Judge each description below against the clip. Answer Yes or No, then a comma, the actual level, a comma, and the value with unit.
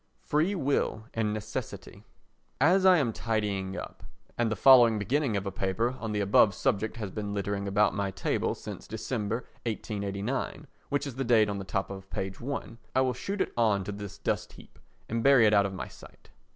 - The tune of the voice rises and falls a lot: No, average, 3.9 semitones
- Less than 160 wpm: No, average, 200 wpm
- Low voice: Yes, low, 110 Hz